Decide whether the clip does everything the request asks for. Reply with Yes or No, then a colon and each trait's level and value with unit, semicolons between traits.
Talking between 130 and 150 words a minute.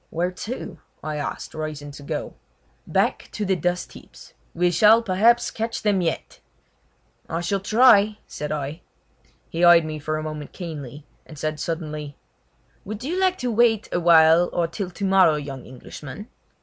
No: average, 160 wpm